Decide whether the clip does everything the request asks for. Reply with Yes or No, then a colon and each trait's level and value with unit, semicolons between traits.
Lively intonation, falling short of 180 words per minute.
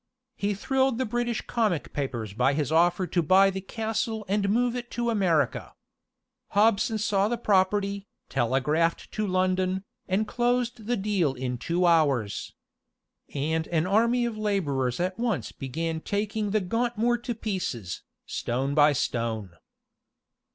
Yes: wide, 6.3 semitones; average, 140 wpm